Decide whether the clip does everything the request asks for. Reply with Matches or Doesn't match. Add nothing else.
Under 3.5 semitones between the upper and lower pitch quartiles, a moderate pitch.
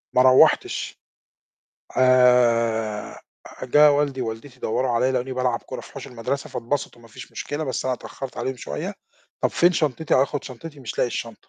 Doesn't match